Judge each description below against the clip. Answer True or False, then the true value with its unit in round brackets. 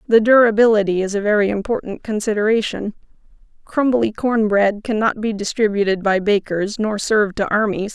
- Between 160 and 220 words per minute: False (145 wpm)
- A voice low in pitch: False (210 Hz)